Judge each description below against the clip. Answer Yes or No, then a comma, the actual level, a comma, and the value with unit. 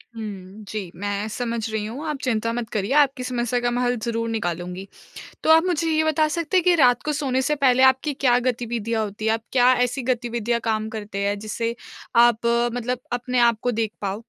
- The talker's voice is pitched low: No, high, 235 Hz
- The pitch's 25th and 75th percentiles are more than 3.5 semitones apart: No, average, 2.7 semitones